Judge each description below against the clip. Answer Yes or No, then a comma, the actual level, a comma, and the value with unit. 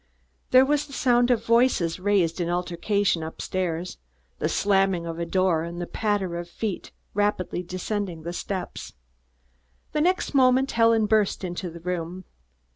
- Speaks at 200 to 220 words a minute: No, average, 155 wpm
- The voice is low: No, high, 190 Hz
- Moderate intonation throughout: Yes, average, 4.5 semitones